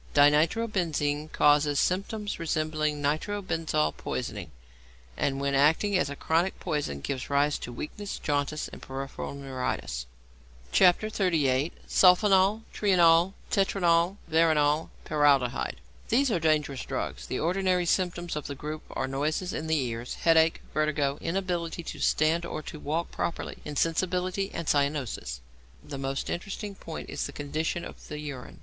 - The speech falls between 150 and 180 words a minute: No, slow, 135 wpm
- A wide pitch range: No, average, 3.8 semitones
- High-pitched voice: No, medium, 155 Hz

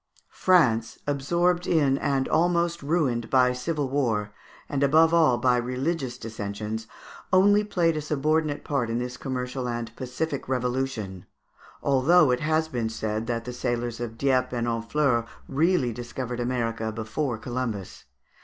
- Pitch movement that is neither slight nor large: Yes, average, 4.4 semitones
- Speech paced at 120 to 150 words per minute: Yes, average, 140 wpm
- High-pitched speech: No, low, 130 Hz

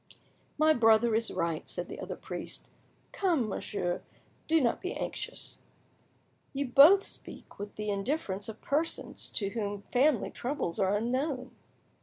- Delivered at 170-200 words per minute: No, average, 140 wpm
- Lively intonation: Yes, wide, 6.0 semitones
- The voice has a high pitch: Yes, high, 235 Hz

